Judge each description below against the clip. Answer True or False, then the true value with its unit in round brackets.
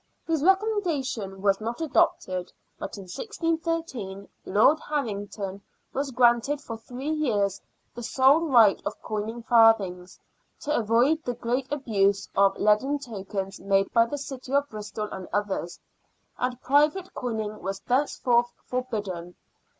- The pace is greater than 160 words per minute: False (135 wpm)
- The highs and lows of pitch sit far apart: True (5.8 semitones)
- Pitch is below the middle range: False (235 Hz)